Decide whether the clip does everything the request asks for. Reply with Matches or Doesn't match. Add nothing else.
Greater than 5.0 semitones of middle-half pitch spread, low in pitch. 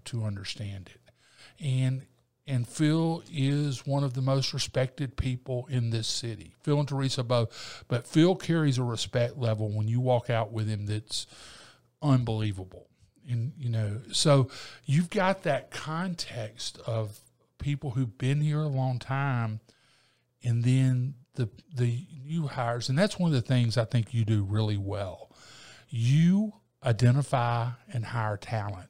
Doesn't match